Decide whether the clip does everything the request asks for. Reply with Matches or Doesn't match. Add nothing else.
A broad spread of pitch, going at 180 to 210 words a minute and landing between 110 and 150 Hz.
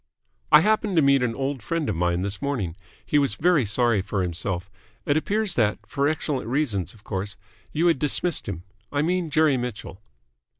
Matches